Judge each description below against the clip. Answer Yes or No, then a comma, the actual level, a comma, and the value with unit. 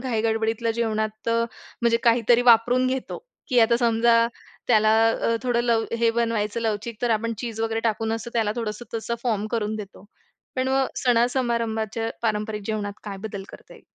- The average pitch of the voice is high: Yes, high, 225 Hz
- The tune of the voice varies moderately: No, narrow, 1.4 semitones